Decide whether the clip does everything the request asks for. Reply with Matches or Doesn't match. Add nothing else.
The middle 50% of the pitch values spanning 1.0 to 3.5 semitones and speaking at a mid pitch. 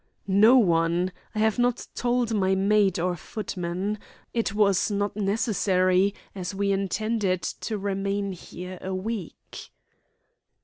Doesn't match